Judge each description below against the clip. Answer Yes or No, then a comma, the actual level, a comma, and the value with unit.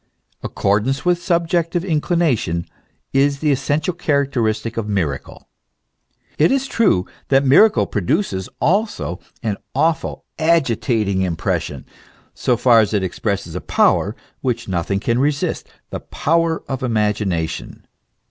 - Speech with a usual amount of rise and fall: No, wide, 8.0 semitones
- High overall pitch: No, low, 130 Hz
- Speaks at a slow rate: Yes, slow, 125 wpm